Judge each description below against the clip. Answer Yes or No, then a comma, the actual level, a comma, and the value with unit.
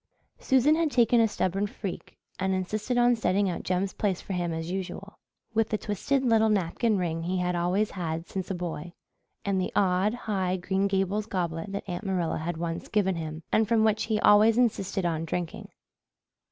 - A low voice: No, high, 190 Hz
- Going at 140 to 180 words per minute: No, average, 190 wpm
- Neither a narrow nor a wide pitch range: Yes, average, 3.4 semitones